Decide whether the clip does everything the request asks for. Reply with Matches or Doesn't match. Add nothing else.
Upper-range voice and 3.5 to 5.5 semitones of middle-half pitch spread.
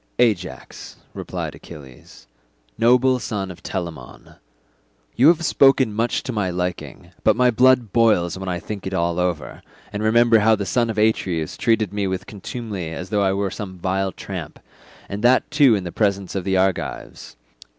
Doesn't match